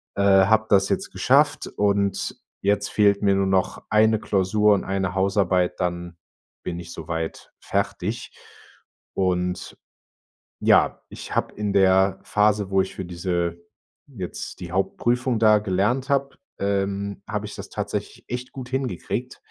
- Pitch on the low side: Yes, low, 100 Hz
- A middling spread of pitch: No, narrow, 2.3 semitones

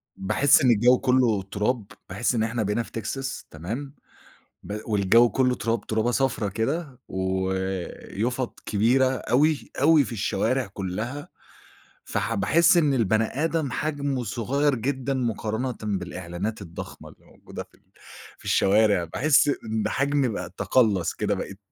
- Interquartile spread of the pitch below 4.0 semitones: No, average, 4.7 semitones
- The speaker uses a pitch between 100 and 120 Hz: Yes, low, 115 Hz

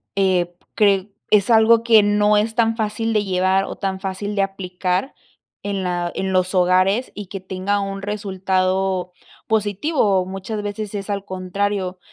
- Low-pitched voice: No, high, 195 Hz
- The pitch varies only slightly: Yes, narrow, 1.9 semitones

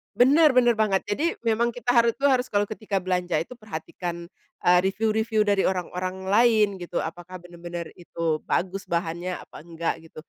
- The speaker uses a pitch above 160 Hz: Yes, high, 190 Hz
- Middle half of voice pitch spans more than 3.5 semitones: Yes, average, 4.4 semitones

